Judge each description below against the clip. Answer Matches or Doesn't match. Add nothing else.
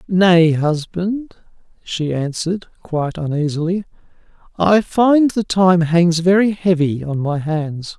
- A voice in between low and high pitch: Matches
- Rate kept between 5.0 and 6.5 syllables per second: Doesn't match